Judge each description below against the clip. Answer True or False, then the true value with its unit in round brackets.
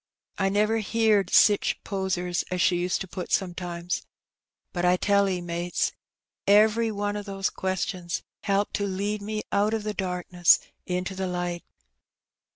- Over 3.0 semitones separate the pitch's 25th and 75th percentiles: False (2.4 semitones)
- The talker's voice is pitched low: False (190 Hz)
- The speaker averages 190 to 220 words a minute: False (155 wpm)